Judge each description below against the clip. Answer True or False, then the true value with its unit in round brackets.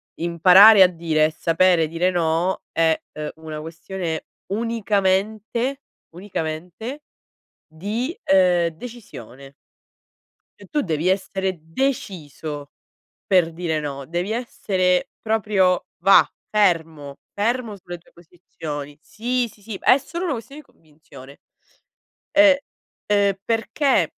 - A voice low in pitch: False (185 Hz)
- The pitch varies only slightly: False (5.3 semitones)